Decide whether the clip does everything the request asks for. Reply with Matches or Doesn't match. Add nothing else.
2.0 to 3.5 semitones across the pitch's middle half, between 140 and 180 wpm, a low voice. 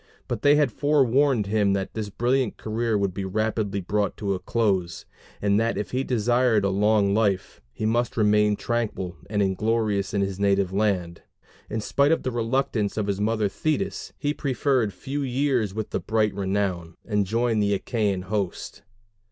Matches